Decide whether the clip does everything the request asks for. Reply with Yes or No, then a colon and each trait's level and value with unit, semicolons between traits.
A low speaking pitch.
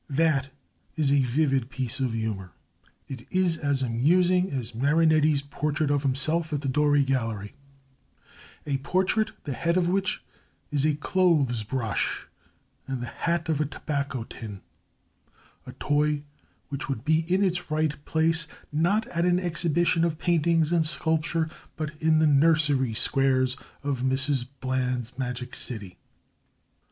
No: medium, 145 Hz